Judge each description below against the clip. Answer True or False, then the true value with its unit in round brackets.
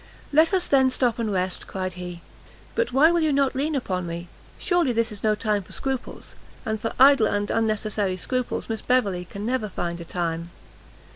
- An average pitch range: False (6.1 semitones)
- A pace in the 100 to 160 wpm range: False (195 wpm)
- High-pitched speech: True (220 Hz)